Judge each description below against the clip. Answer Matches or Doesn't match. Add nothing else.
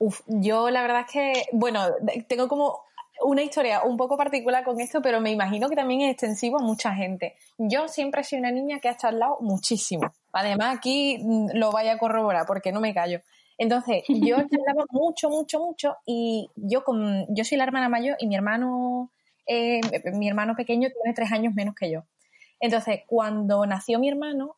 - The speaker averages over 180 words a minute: Matches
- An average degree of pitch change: Matches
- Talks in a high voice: Matches